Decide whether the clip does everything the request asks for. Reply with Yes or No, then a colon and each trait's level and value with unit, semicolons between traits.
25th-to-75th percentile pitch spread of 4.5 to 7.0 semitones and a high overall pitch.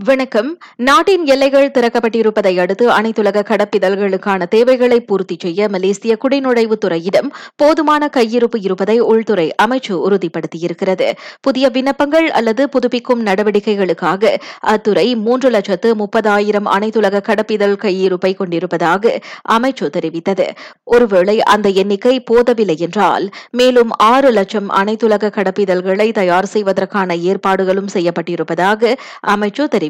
No: average, 4.1 semitones; high, 210 Hz